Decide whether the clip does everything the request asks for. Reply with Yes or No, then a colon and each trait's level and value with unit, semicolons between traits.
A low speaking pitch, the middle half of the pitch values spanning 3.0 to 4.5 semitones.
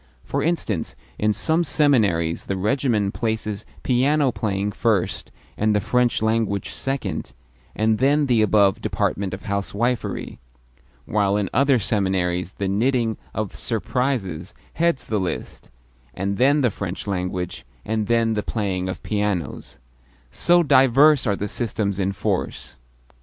Yes: low, 105 Hz; average, 4.2 semitones